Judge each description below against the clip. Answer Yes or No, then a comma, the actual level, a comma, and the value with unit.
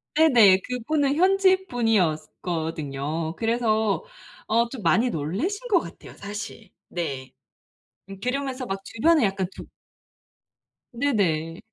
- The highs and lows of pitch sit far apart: Yes, wide, 8.6 semitones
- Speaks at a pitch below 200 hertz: No, high, 220 Hz